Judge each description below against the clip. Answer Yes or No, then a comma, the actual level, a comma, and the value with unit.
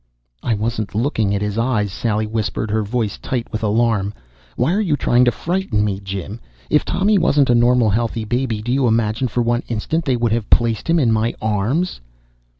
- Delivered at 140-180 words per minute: No, average, 200 wpm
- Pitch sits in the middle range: No, low, 115 Hz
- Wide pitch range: No, average, 2.9 semitones